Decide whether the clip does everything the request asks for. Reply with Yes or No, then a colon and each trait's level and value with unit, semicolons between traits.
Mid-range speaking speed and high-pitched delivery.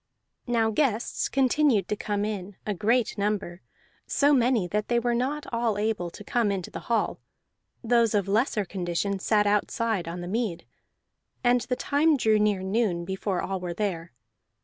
Yes: average, 170 wpm; high, 210 Hz